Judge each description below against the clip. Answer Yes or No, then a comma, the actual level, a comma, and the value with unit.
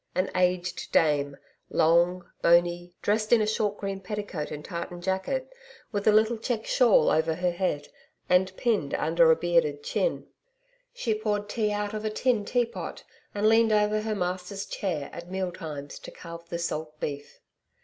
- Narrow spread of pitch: No, average, 4.0 semitones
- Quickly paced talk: No, average, 170 wpm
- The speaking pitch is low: No, high, 195 Hz